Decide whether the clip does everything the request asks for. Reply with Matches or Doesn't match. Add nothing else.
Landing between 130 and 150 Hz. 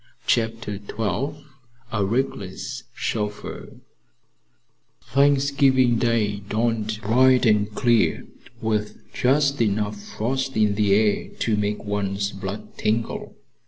Doesn't match